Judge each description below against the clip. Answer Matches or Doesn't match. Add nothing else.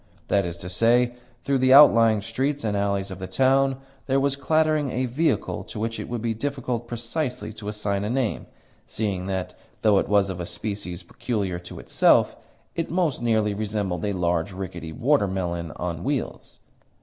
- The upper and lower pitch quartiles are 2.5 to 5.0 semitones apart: Doesn't match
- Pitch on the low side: Matches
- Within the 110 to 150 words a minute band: Doesn't match